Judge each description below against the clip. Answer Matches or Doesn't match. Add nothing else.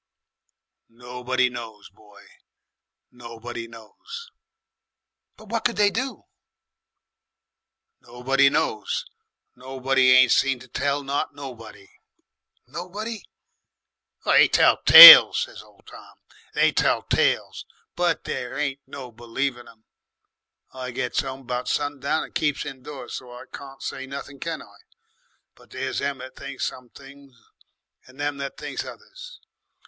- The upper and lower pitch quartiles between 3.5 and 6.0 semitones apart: Doesn't match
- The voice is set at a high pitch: Doesn't match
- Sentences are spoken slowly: Matches